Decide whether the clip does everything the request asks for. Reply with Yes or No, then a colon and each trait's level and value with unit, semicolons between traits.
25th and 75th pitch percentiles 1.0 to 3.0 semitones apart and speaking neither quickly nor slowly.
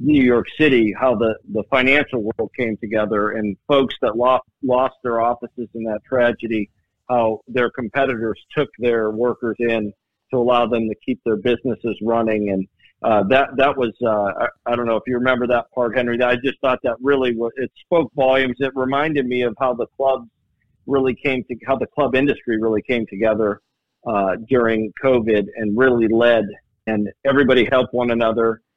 Yes: average, 2.7 semitones; average, 185 wpm